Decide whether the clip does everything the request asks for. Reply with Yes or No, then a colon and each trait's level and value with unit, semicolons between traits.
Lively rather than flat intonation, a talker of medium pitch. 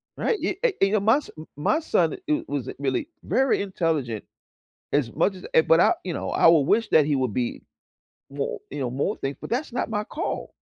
Yes: wide, 8.6 semitones; medium, 165 Hz